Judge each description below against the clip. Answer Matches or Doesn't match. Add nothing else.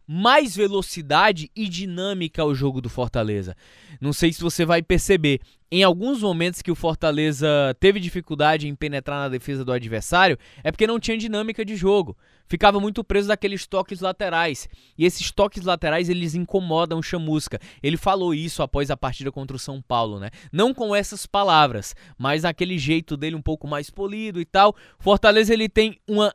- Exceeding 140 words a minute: Matches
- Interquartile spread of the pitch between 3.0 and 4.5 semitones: Doesn't match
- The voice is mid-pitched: Matches